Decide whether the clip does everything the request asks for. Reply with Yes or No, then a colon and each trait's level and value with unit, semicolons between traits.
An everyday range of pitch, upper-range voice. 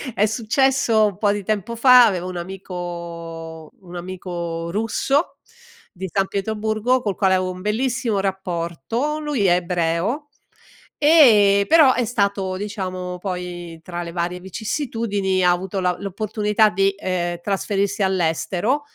Yes: average, 3.6 semitones; high, 195 Hz